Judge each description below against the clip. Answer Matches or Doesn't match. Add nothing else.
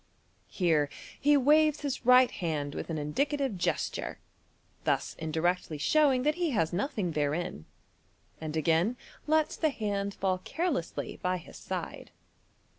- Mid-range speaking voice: Doesn't match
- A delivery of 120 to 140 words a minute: Matches